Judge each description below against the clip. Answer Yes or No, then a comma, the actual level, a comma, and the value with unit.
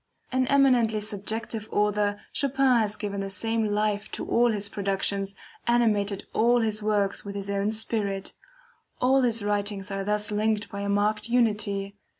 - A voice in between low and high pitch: No, high, 210 Hz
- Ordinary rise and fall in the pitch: No, narrow, 2.0 semitones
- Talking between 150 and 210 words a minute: Yes, average, 155 wpm